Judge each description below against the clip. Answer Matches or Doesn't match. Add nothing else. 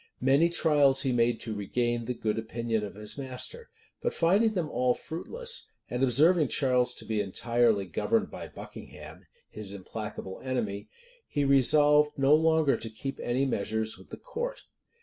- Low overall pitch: Matches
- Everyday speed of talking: Matches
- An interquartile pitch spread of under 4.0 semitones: Doesn't match